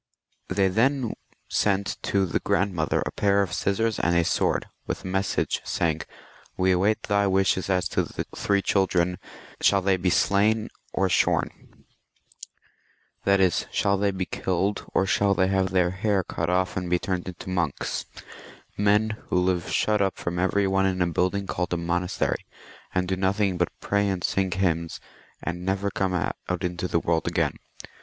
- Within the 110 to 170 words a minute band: No, average, 180 wpm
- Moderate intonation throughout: No, narrow, 1.8 semitones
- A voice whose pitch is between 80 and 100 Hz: Yes, very low, 95 Hz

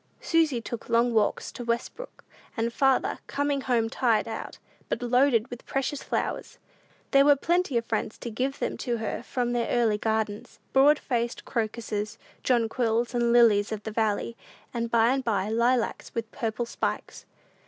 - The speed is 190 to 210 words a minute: No, average, 165 wpm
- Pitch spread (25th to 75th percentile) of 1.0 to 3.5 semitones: Yes, narrow, 2.4 semitones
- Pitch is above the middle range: Yes, high, 235 Hz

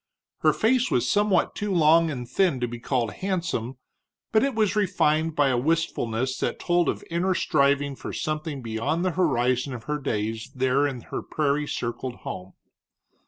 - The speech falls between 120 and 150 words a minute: No, average, 170 wpm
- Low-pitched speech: No, medium, 145 Hz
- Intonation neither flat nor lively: No, wide, 5.8 semitones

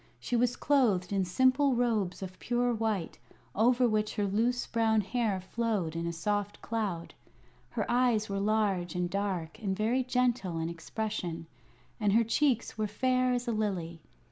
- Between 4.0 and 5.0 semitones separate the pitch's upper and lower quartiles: Yes, average, 4.3 semitones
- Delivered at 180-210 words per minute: No, average, 165 wpm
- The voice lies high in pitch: Yes, high, 215 Hz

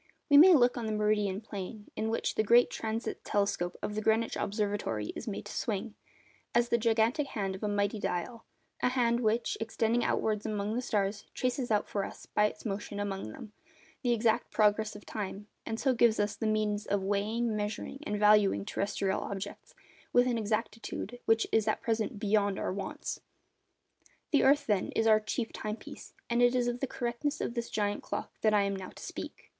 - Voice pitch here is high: Yes, high, 215 Hz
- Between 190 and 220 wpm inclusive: Yes, average, 200 wpm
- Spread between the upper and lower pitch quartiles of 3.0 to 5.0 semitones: No, narrow, 2.4 semitones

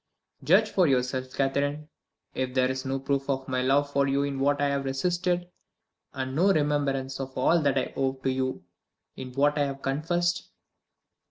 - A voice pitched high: No, medium, 140 Hz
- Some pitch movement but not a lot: No, narrow, 1.8 semitones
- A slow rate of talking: No, average, 180 wpm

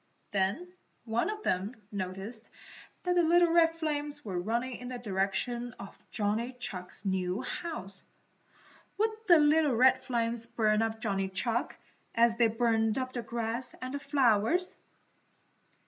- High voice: Yes, high, 235 Hz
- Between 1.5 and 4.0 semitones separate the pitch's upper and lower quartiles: No, average, 5.1 semitones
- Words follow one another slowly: No, average, 145 wpm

